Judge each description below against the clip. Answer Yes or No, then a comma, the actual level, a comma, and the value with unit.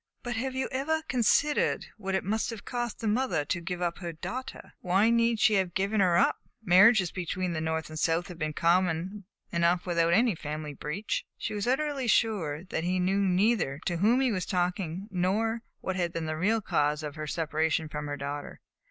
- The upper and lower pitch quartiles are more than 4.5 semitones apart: Yes, average, 5.1 semitones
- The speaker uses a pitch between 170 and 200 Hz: Yes, medium, 185 Hz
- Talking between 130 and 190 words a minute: No, fast, 205 wpm